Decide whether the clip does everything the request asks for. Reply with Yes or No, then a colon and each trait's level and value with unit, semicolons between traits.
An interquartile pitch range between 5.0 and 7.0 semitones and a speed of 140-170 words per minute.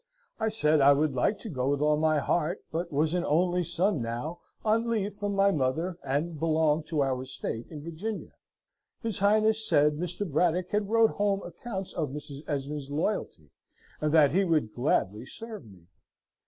No: wide, 5.5 semitones; average, 180 wpm